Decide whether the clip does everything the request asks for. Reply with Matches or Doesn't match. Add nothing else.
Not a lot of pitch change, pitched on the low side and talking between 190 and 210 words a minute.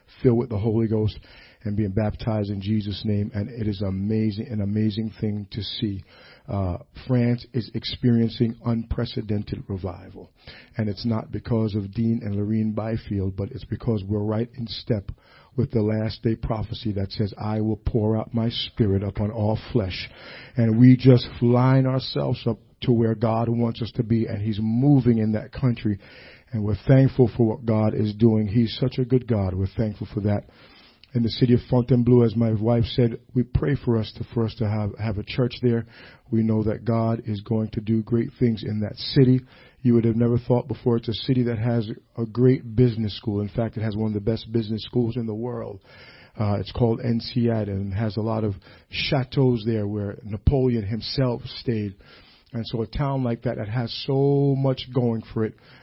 Matches